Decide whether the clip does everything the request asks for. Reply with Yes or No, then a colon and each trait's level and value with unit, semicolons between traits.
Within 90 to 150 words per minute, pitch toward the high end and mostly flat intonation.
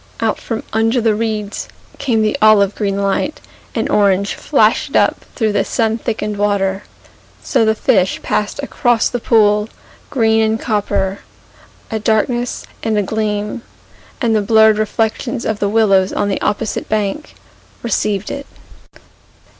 Yes: average, 145 wpm; high, 215 Hz; narrow, 1.6 semitones